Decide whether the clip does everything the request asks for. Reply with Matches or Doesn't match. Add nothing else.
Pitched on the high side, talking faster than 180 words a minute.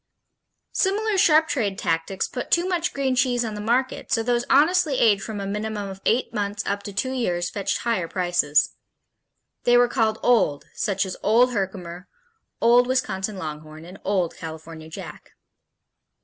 Doesn't match